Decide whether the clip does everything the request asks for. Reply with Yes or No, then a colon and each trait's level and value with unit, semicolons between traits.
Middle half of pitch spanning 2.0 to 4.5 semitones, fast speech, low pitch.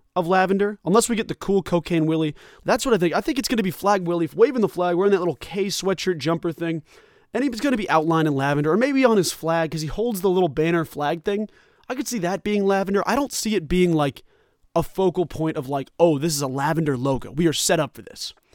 No: average, 4.2 semitones; fast, 260 wpm; medium, 180 Hz